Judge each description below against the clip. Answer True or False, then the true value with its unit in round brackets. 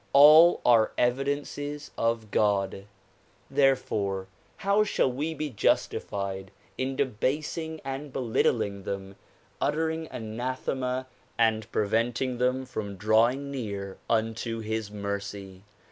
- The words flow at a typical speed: False (100 wpm)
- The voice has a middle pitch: False (120 Hz)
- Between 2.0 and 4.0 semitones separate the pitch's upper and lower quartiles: False (5.0 semitones)